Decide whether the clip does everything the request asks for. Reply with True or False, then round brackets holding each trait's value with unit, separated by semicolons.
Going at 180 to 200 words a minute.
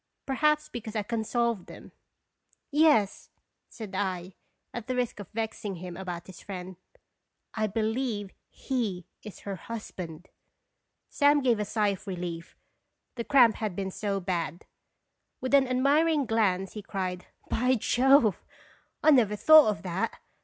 False (150 wpm)